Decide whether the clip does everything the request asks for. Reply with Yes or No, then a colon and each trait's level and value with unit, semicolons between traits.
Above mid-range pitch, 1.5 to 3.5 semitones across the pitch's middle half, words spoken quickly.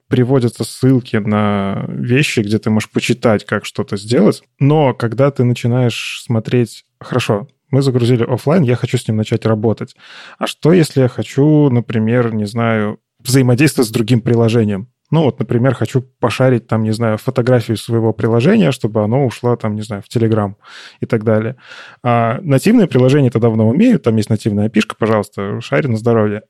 No: low, 120 Hz; average, 2.8 semitones; fast, 170 wpm